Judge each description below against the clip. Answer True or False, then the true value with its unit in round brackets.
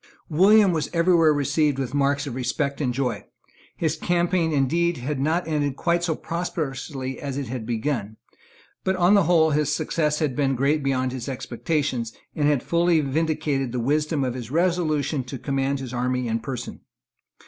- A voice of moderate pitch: True (145 Hz)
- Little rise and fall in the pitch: False (3.7 semitones)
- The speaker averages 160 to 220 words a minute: True (170 wpm)